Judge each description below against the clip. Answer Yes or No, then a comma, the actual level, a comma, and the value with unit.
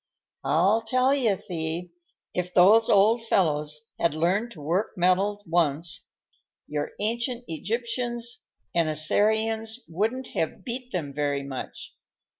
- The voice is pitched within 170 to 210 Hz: Yes, high, 190 Hz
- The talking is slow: Yes, slow, 120 wpm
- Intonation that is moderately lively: No, wide, 6.0 semitones